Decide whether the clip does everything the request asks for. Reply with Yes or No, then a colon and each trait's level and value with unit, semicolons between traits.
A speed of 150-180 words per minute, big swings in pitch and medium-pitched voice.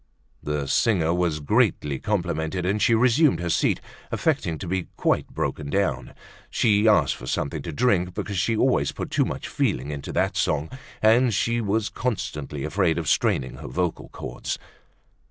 No: average, 165 wpm; wide, 6.0 semitones; very low, 90 Hz